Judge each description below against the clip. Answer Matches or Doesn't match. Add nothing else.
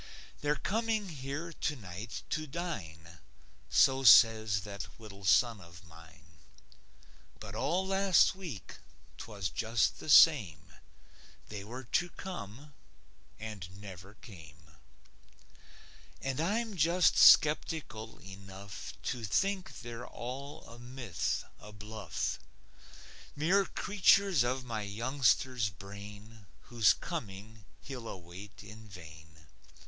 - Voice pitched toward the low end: Matches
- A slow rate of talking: Matches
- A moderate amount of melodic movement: Doesn't match